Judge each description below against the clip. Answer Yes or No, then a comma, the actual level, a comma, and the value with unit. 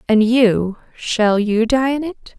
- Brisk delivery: No, average, 150 wpm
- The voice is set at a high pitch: Yes, high, 235 Hz